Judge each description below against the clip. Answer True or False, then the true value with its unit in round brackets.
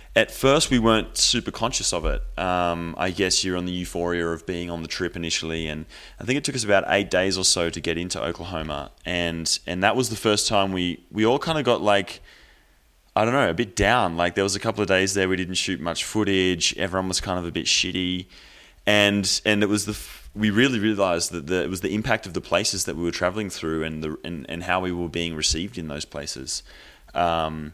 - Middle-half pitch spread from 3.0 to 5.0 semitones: True (3.3 semitones)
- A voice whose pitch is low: True (90 Hz)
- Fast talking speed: True (240 wpm)